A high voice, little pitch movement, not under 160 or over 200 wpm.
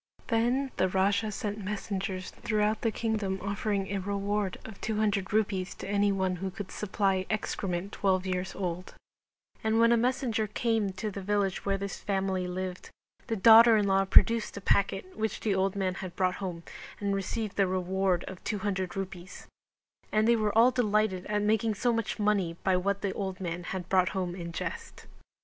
Yes: high, 200 Hz; narrow, 2.3 semitones; average, 180 wpm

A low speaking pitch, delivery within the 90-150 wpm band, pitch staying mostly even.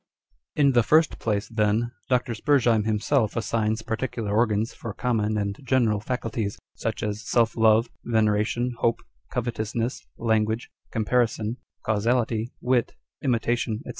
Yes: low, 115 Hz; slow, 135 wpm; narrow, 2.0 semitones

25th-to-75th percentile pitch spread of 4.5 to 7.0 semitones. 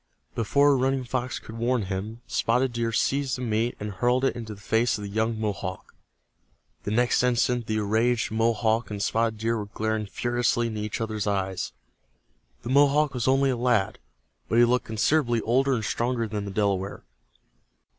No: narrow, 2.6 semitones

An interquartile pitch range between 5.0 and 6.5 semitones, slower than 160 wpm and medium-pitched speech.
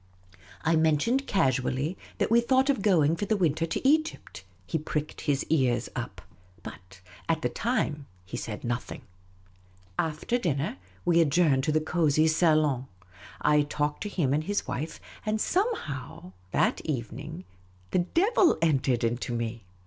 Yes: wide, 5.6 semitones; average, 150 wpm; medium, 155 Hz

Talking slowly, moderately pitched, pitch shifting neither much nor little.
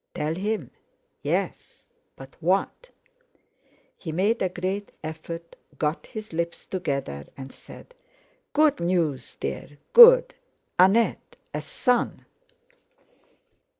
No: slow, 90 wpm; medium, 175 Hz; wide, 5.7 semitones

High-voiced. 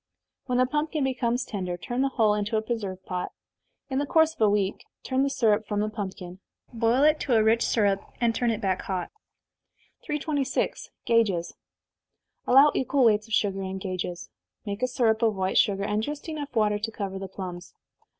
Yes: high, 220 Hz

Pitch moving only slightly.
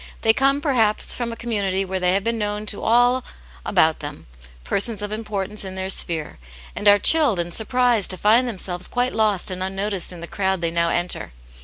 No: average, 3.7 semitones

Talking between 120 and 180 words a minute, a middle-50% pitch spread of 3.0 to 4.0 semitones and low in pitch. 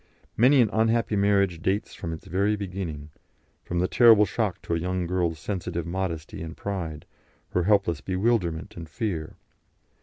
Yes: average, 155 wpm; average, 3.7 semitones; very low, 95 Hz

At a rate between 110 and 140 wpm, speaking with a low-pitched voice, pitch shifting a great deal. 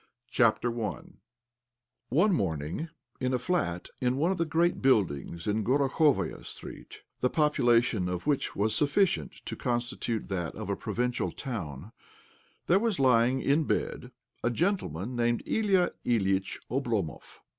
Yes: slow, 135 wpm; low, 125 Hz; wide, 6.5 semitones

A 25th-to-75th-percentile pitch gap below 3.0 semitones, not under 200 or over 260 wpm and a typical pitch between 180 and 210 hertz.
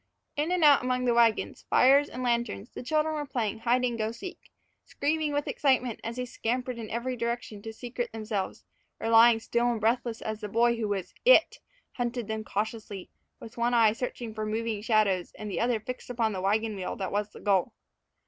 No: narrow, 2.5 semitones; fast, 205 wpm; high, 235 Hz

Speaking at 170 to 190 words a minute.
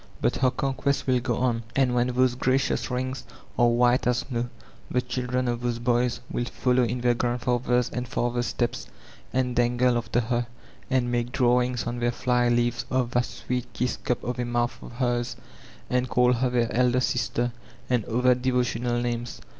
Yes: average, 185 wpm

